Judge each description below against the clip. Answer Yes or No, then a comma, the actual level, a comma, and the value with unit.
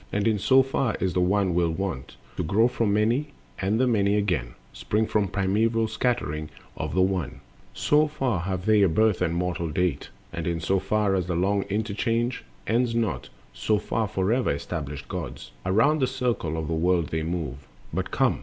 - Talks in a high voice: No, low, 100 Hz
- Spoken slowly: No, average, 190 wpm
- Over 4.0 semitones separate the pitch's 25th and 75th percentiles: Yes, average, 4.6 semitones